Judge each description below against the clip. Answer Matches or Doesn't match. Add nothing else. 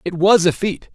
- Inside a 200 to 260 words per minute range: Matches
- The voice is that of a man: Matches